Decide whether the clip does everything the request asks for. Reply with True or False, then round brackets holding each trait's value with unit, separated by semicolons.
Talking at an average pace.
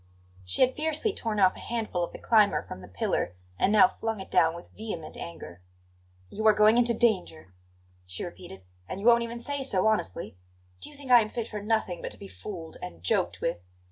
False (215 wpm)